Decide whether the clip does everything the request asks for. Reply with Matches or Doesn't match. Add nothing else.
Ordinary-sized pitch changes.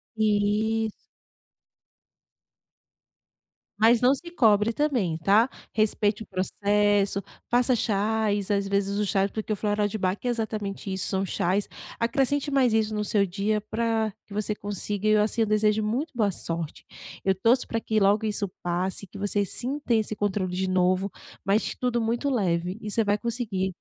Doesn't match